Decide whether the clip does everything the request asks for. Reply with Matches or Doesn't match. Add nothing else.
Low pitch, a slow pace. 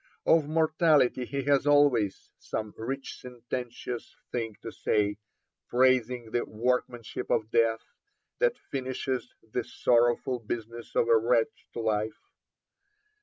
Matches